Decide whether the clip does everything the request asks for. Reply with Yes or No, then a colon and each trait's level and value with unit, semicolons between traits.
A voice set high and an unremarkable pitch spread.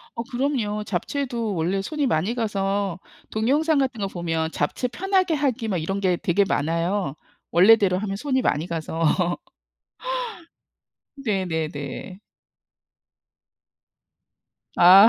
No: high, 200 Hz; wide, 5.7 semitones